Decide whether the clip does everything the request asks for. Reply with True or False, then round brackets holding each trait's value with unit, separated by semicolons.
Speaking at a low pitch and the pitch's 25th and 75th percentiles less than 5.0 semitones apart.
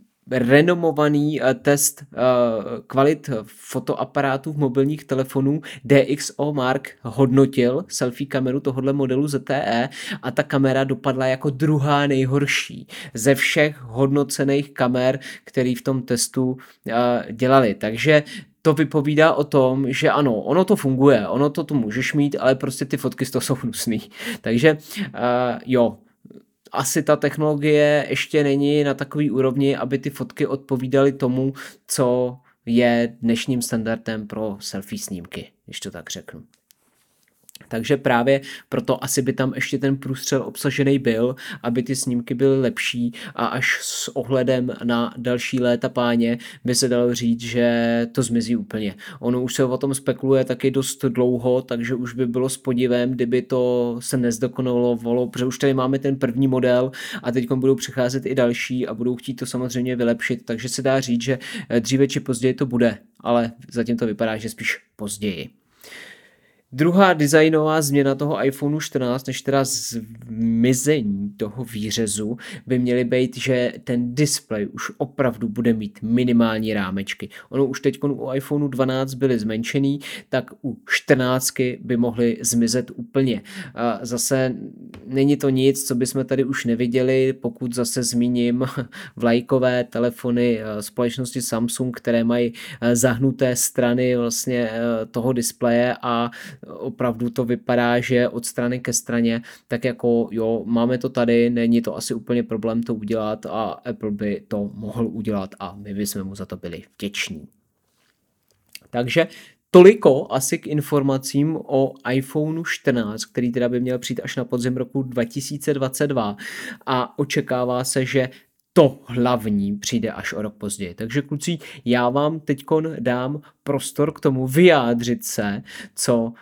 True (130 Hz; 2.5 semitones)